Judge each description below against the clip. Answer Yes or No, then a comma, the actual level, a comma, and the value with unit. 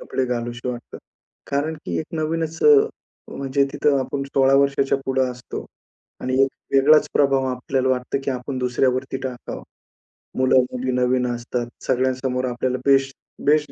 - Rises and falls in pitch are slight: Yes, narrow, 1.6 semitones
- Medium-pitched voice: No, low, 130 Hz